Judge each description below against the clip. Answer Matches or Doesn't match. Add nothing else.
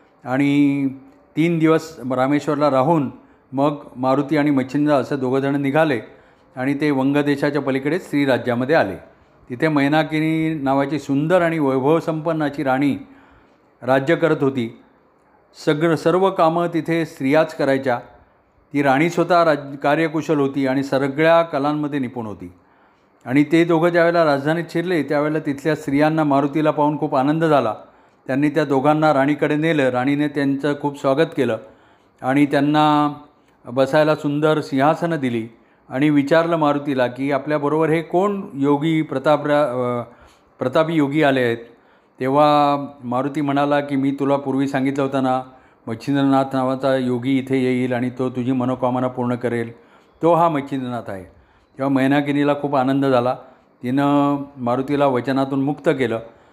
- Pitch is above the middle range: Doesn't match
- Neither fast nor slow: Doesn't match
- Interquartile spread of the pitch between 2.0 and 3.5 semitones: Matches